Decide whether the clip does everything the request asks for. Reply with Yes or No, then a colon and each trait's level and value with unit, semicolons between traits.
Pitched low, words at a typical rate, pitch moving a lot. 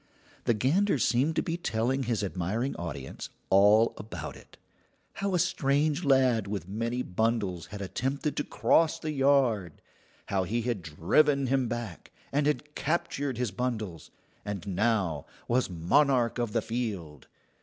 Yes: low, 120 Hz; average, 145 wpm; wide, 5.7 semitones